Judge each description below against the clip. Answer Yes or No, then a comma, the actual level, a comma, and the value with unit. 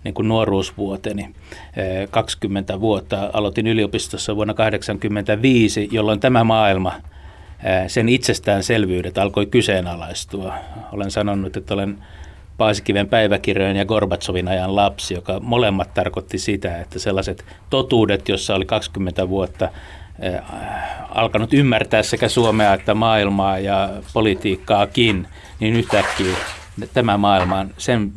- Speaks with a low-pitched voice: Yes, low, 100 Hz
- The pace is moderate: Yes, average, 110 wpm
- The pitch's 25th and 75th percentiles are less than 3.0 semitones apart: Yes, narrow, 2.6 semitones